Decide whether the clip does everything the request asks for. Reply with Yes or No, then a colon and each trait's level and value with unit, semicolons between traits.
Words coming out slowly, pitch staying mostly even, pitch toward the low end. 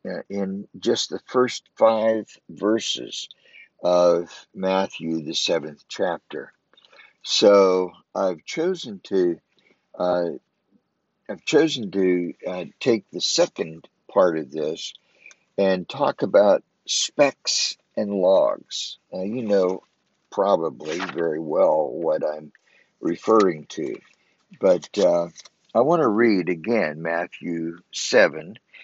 No: slow, 105 wpm; average, 3.8 semitones; very low, 90 Hz